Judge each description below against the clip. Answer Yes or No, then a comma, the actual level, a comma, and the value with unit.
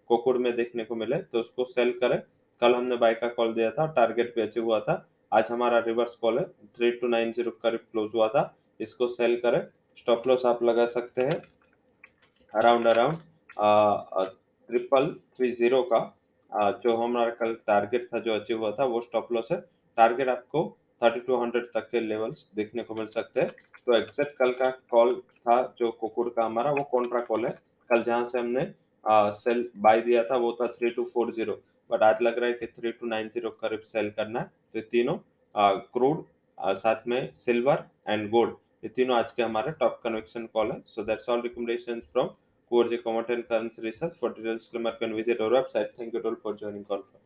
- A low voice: Yes, low, 120 Hz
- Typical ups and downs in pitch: No, narrow, 1.3 semitones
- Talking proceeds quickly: No, average, 185 wpm